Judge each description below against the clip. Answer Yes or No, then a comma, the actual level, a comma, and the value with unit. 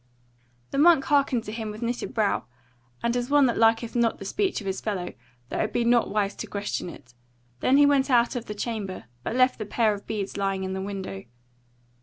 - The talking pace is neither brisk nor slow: No, fast, 220 wpm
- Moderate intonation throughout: Yes, average, 3.6 semitones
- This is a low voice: No, high, 225 Hz